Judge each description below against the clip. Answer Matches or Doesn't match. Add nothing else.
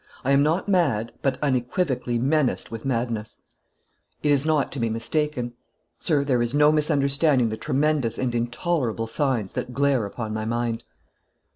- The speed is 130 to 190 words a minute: Matches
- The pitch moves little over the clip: Doesn't match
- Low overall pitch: Matches